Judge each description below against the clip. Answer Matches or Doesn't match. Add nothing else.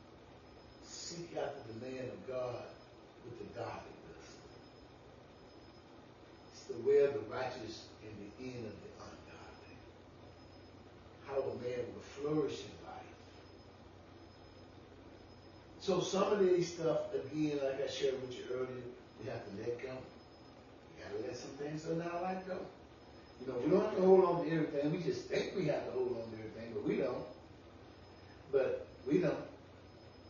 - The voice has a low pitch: Matches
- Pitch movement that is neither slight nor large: Doesn't match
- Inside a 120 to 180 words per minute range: Matches